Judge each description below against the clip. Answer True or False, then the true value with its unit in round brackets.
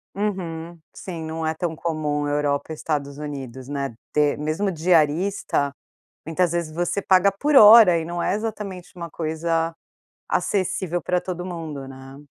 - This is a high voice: False (165 Hz)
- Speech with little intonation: False (3.6 semitones)